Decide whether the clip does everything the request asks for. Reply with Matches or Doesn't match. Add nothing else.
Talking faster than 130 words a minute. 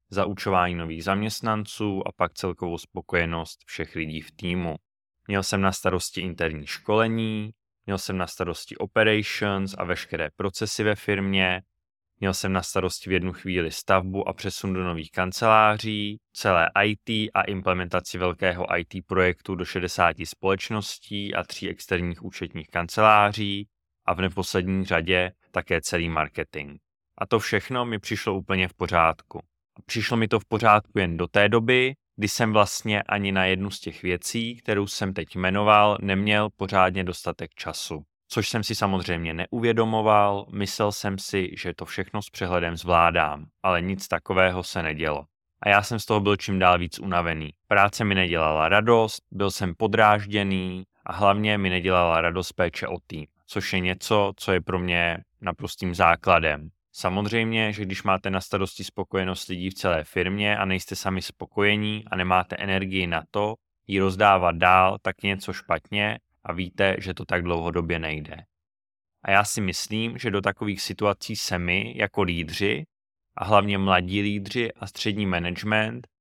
Matches